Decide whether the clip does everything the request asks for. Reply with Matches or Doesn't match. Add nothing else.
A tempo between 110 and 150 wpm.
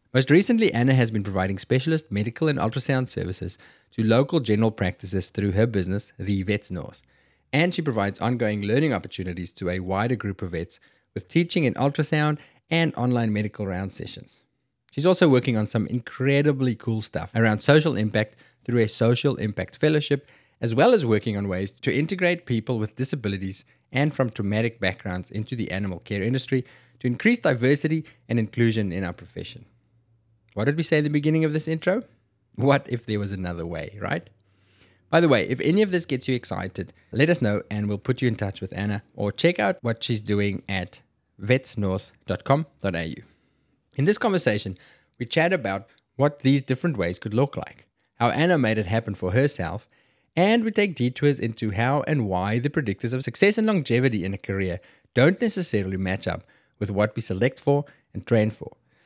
Doesn't match